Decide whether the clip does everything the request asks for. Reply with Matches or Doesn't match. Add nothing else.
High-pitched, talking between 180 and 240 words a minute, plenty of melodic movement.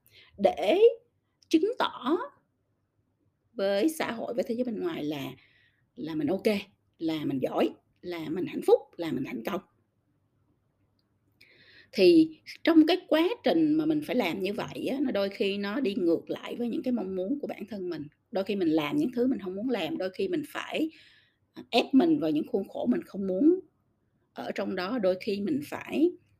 Matches